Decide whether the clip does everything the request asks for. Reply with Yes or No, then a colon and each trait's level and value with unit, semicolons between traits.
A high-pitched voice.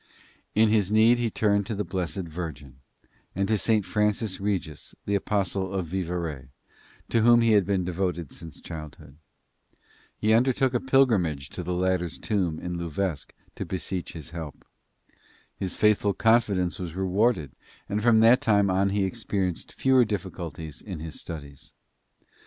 No: very low, 95 Hz